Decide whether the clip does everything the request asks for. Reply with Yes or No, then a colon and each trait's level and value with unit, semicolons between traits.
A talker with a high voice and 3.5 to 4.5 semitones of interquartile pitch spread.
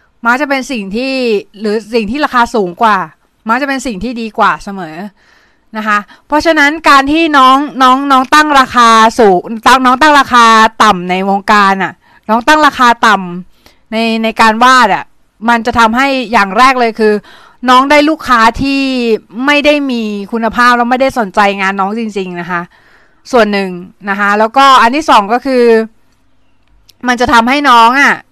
Yes: high, 235 Hz; average, 3.8 semitones